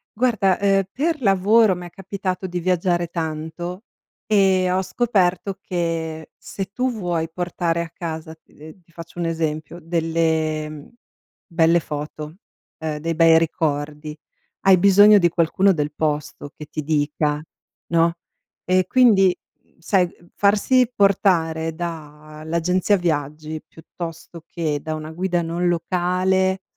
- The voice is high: No, medium, 170 Hz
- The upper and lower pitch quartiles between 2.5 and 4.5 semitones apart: Yes, average, 2.9 semitones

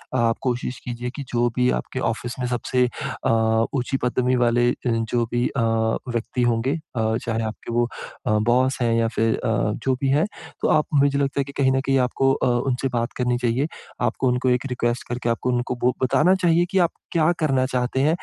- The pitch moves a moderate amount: No, narrow, 2.1 semitones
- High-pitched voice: No, low, 125 Hz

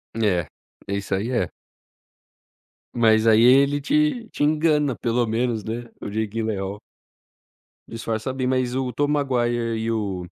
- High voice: No, low, 120 Hz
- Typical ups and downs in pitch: Yes, average, 3.3 semitones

